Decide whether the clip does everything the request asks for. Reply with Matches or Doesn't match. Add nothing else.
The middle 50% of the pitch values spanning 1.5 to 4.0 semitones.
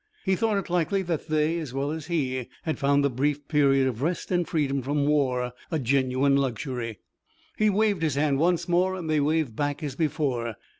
Matches